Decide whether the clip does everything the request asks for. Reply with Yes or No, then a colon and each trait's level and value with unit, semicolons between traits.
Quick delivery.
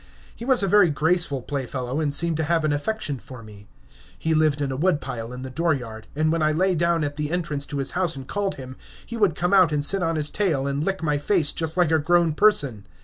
Yes: fast, 255 wpm